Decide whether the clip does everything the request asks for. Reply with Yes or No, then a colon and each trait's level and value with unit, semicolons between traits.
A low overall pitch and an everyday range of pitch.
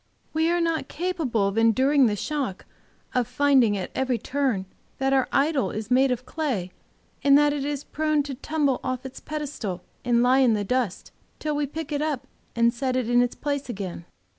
No: very high, 265 Hz; average, 3.7 semitones